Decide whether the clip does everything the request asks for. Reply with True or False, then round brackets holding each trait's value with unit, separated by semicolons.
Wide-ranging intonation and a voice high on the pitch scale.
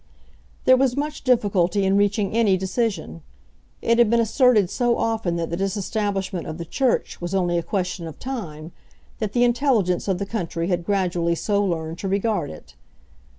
False (4.8 semitones; 195 Hz)